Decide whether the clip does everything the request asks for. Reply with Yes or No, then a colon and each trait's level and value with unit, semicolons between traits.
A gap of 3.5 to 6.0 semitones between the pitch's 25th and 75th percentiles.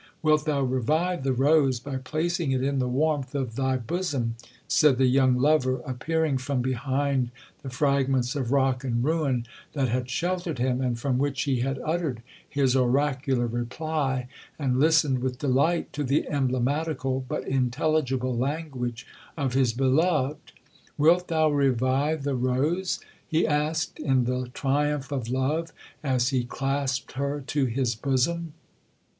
No: average, 2.8 semitones